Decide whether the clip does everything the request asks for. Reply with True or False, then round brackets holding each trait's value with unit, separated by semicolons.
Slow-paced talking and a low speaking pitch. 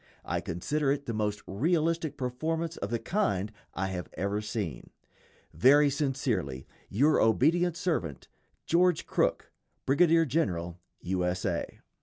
True (130 wpm; 125 Hz)